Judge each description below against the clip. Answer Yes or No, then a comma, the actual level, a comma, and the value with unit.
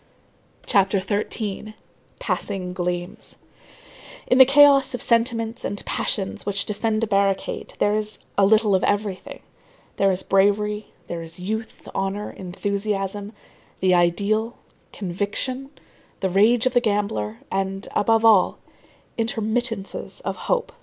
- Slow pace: Yes, slow, 120 wpm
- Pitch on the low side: No, high, 205 Hz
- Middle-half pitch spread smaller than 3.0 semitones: Yes, narrow, 2.6 semitones